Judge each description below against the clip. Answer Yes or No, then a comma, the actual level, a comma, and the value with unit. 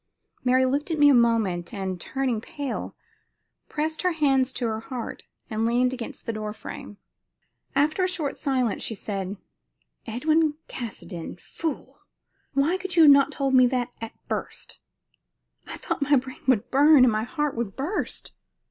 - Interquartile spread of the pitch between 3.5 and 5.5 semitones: Yes, average, 4.4 semitones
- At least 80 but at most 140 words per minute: No, average, 160 wpm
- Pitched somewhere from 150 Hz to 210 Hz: No, very high, 260 Hz